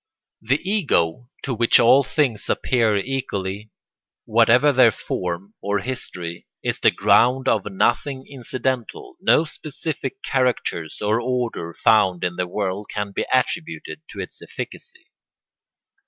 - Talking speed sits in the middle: No, slow, 125 wpm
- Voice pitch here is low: Yes, low, 120 Hz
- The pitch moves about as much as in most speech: Yes, average, 5.0 semitones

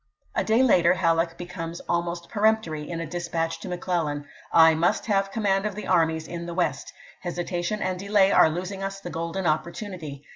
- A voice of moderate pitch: Yes, medium, 175 Hz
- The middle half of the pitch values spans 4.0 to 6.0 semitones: No, average, 2.9 semitones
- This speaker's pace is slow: No, average, 185 wpm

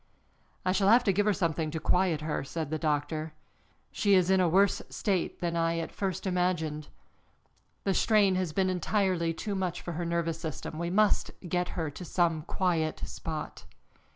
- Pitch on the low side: No, medium, 175 Hz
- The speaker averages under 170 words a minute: No, average, 180 wpm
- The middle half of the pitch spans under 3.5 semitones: Yes, average, 2.9 semitones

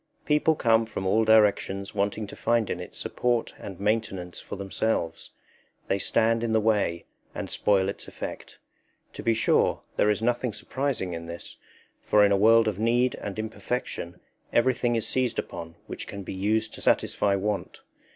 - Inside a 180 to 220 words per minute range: No, average, 170 wpm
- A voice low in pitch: Yes, low, 105 Hz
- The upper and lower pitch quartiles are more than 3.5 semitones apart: No, average, 2.7 semitones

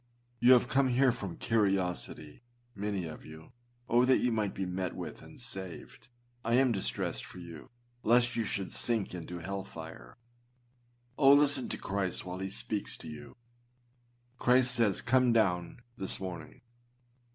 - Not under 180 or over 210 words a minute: No, average, 160 wpm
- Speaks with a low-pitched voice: Yes, low, 100 Hz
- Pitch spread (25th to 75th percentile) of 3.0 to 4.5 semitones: No, average, 5.3 semitones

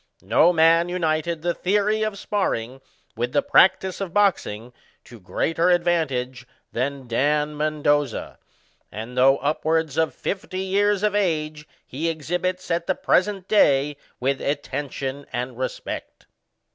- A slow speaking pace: Yes, slow, 130 wpm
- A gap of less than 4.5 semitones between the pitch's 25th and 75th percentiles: No, average, 5.3 semitones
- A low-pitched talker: No, medium, 155 Hz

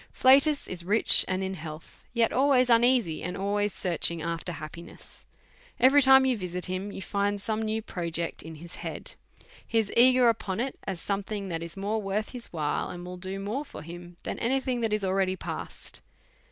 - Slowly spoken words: No, average, 195 wpm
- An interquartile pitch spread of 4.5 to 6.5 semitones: Yes, average, 4.8 semitones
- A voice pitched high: Yes, high, 200 Hz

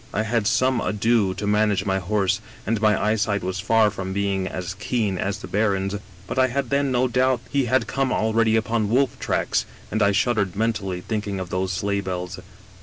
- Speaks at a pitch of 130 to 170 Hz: No, low, 105 Hz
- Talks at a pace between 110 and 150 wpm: No, average, 195 wpm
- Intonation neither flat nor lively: Yes, average, 3.0 semitones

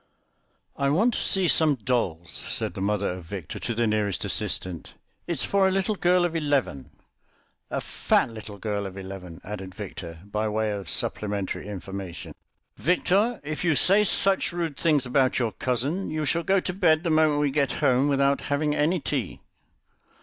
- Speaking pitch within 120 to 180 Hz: Yes, low, 135 Hz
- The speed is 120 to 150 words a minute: No, average, 175 wpm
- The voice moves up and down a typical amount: No, wide, 8.4 semitones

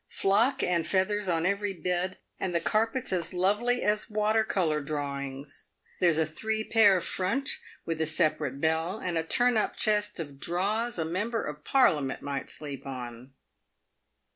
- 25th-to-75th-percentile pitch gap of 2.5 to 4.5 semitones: No, average, 5.3 semitones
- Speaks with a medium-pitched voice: Yes, medium, 180 Hz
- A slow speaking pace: No, average, 160 wpm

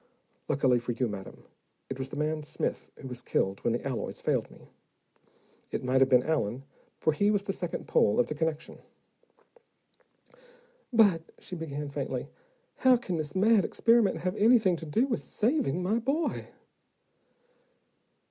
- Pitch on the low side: No, medium, 160 Hz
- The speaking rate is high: No, average, 155 wpm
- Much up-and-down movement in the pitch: Yes, wide, 7.7 semitones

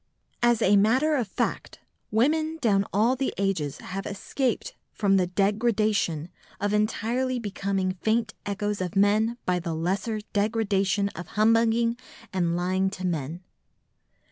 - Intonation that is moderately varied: Yes, average, 3.3 semitones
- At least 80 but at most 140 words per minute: Yes, slow, 135 wpm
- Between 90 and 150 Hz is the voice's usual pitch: No, high, 205 Hz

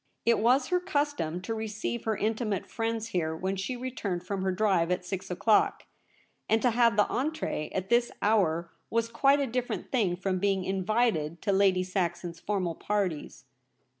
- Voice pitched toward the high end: Yes, high, 205 Hz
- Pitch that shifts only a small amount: No, average, 4.2 semitones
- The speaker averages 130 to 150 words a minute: No, average, 175 wpm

